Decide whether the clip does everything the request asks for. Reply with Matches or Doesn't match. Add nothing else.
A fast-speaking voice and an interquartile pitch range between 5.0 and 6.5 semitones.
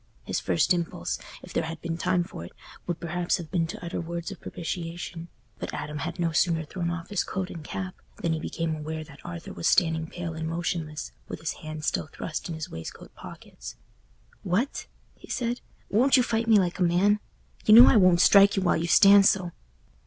Doesn't match